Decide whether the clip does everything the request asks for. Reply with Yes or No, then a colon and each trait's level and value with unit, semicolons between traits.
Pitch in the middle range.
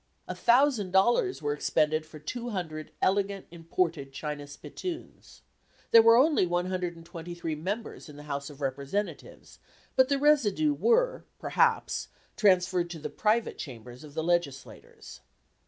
Yes: medium, 175 Hz